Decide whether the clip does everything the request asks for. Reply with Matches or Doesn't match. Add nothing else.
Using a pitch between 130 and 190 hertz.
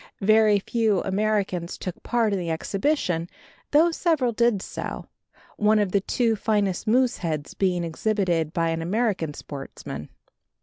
Doesn't match